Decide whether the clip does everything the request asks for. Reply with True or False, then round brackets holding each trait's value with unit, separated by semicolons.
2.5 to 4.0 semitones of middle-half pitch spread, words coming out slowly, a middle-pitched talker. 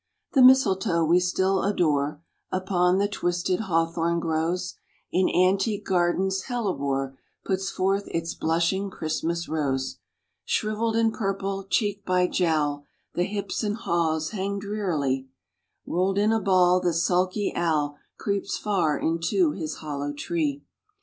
True (3.4 semitones; 130 wpm; 180 Hz)